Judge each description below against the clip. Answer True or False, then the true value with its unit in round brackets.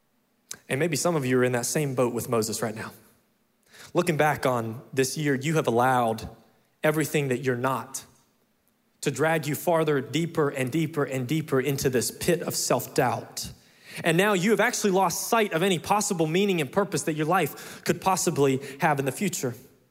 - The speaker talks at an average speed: True (190 wpm)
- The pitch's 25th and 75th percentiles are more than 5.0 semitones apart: True (5.4 semitones)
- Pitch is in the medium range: True (150 Hz)